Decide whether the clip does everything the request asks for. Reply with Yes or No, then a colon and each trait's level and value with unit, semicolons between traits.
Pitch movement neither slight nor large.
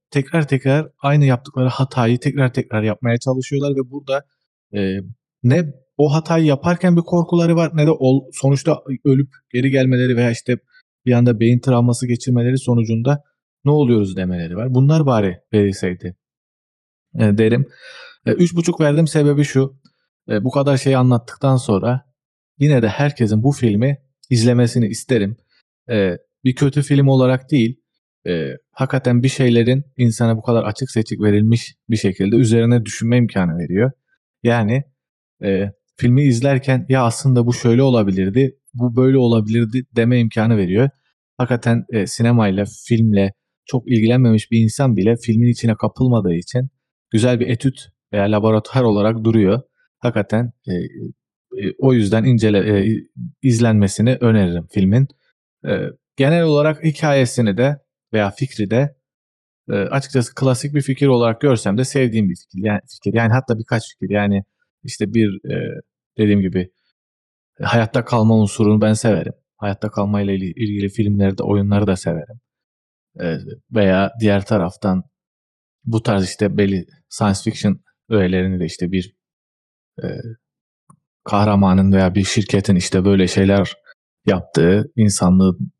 Yes: average, 4.4 semitones